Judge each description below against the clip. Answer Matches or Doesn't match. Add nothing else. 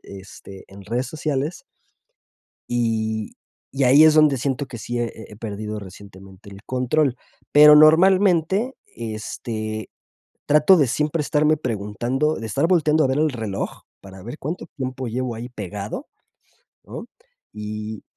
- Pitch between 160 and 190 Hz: Doesn't match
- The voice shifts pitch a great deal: Matches